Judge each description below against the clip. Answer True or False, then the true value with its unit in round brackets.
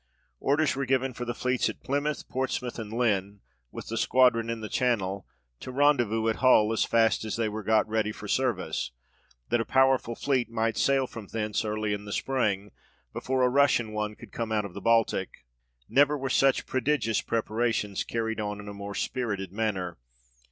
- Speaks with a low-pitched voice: True (115 Hz)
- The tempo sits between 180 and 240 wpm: True (190 wpm)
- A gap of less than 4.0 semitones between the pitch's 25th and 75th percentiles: True (3.3 semitones)